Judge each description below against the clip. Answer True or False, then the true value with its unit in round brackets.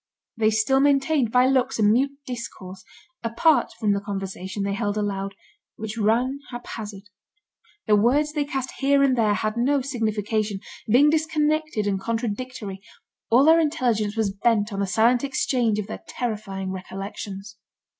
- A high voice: True (225 Hz)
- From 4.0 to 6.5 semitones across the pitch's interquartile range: True (4.4 semitones)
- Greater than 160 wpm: False (150 wpm)